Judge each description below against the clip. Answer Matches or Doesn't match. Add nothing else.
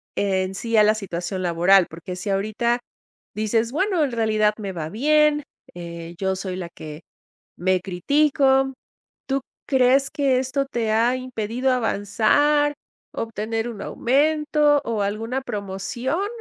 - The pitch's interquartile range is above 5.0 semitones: Matches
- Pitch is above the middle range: Matches